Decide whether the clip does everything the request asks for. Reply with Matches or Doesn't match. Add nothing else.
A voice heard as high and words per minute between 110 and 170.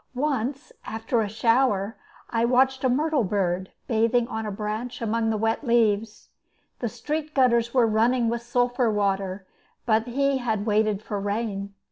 Matches